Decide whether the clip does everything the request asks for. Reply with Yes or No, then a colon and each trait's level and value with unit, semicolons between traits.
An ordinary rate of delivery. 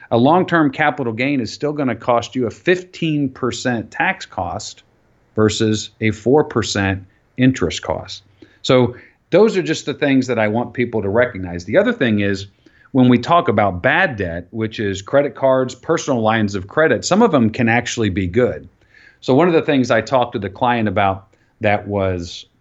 Yes: average, 185 wpm